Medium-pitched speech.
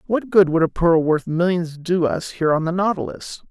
Yes: medium, 170 Hz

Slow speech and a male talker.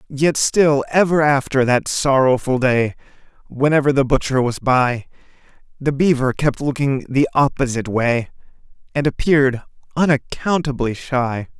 Yes: slow, 120 wpm; male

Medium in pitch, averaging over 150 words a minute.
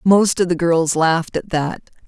Yes: medium, 170 Hz; fast, 205 wpm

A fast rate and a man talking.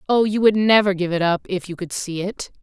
No: fast, 275 wpm; female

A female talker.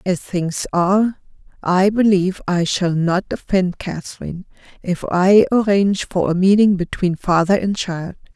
Yes: female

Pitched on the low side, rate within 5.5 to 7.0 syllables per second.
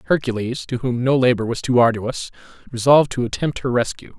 Yes: low, 125 Hz; 5.9 syllables/s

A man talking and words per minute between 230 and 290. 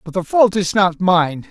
Yes: male; fast, 240 wpm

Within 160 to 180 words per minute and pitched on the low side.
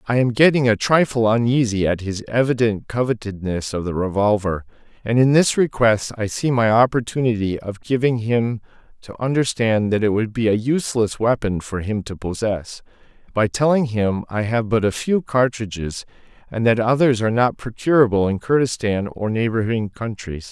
Yes: average, 165 wpm; low, 115 Hz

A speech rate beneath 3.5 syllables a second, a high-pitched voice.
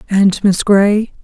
Yes: 3.1 syllables/s; high, 200 Hz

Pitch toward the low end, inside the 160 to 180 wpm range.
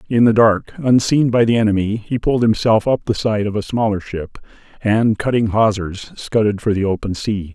No: low, 110 Hz; average, 200 wpm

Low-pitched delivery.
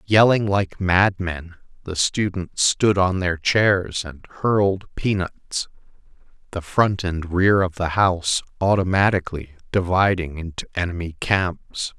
Yes: very low, 90 Hz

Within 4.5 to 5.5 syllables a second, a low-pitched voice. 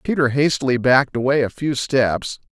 Yes: 5.2 syllables/s; low, 130 Hz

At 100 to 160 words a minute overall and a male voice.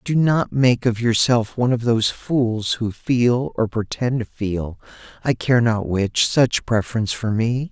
No: average, 180 wpm; male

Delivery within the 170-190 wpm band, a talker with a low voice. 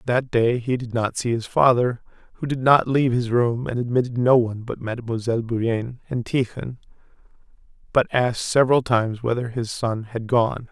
Yes: average, 180 wpm; low, 120 Hz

